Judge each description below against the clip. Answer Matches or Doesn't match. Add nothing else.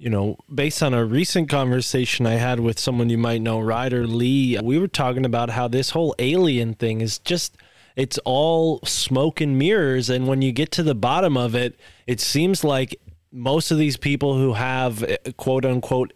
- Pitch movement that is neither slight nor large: Matches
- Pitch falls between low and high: Doesn't match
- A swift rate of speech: Doesn't match